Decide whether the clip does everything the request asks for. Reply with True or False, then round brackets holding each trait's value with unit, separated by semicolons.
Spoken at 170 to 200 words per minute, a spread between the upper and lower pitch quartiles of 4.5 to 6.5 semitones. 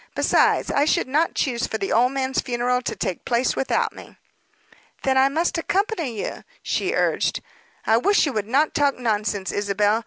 True (180 wpm; 4.9 semitones)